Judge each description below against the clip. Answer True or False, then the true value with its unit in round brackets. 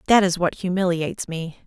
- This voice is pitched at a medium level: True (180 Hz)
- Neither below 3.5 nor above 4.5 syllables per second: False (5.6 syllables/s)